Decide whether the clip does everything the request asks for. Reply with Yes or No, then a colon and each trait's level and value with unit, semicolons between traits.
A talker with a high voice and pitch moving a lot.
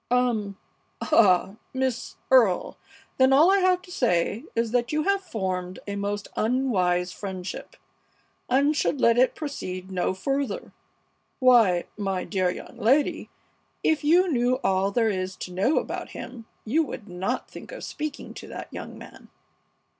Yes: high, 230 Hz; wide, 6.4 semitones